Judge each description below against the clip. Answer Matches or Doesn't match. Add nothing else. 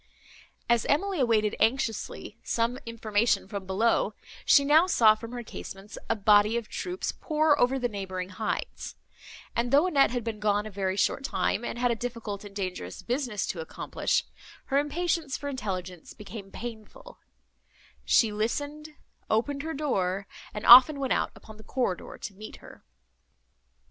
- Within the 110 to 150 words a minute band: Doesn't match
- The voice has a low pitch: Doesn't match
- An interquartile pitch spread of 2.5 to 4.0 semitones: Doesn't match